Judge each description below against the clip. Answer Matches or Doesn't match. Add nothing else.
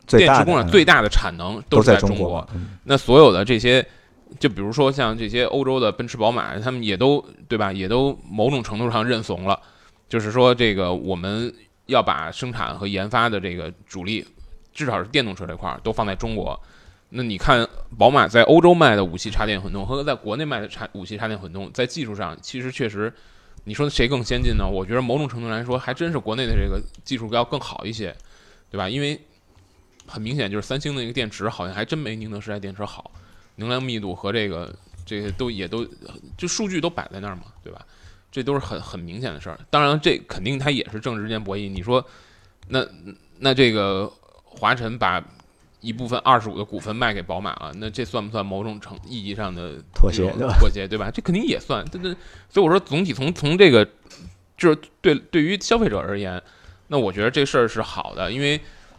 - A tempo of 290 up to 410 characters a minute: Matches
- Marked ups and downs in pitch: Doesn't match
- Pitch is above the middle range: Doesn't match